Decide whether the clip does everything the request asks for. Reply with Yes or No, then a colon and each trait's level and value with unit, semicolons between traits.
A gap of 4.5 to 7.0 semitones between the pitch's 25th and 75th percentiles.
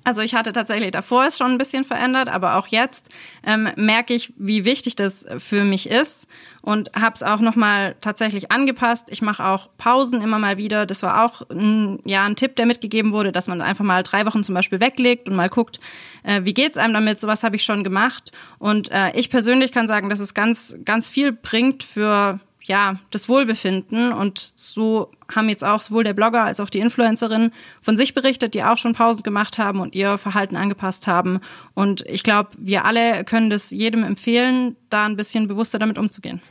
No: average, 2.7 semitones